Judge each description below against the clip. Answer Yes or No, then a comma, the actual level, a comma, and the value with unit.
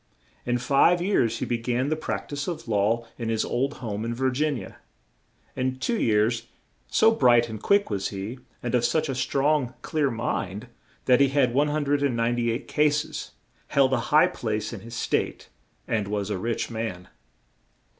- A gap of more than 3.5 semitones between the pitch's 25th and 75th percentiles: Yes, average, 3.9 semitones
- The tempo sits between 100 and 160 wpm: No, average, 175 wpm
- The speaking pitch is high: No, low, 120 Hz